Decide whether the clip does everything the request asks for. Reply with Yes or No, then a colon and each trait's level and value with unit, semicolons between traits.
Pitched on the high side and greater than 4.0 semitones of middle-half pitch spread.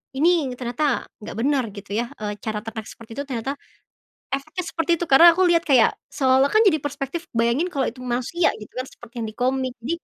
Yes: very high, 265 Hz; average, 4.6 semitones